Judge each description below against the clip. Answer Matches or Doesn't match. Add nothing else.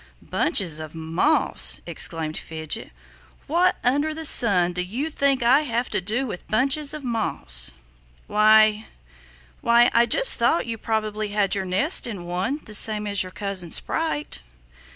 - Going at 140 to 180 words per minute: Matches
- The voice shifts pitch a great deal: Matches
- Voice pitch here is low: Doesn't match